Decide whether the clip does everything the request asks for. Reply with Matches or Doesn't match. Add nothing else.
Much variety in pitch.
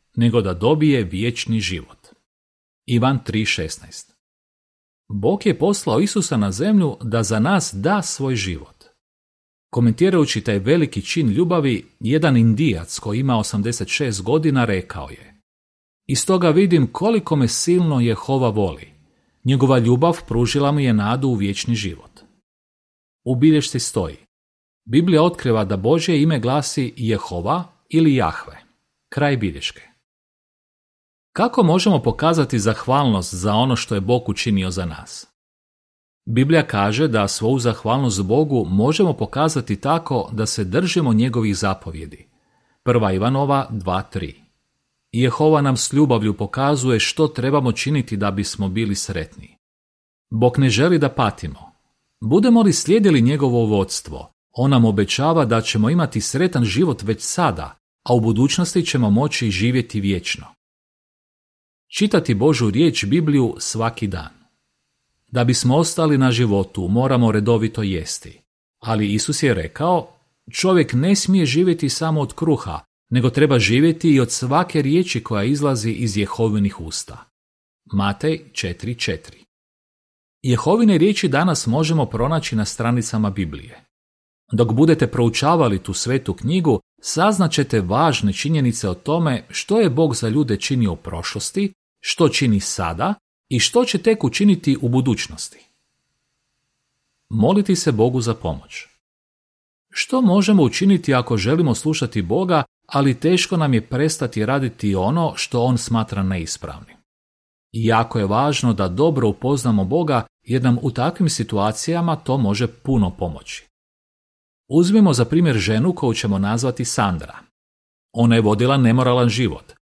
Matches